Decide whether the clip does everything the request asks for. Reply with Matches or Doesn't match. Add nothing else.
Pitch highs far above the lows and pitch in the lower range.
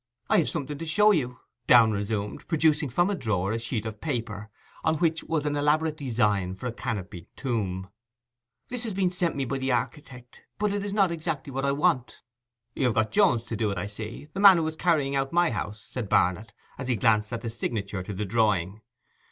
Matches